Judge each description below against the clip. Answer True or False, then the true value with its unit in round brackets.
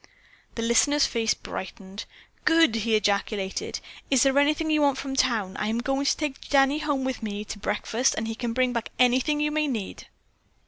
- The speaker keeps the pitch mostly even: False (4.4 semitones)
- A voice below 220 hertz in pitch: False (250 Hz)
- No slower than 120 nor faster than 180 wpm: False (190 wpm)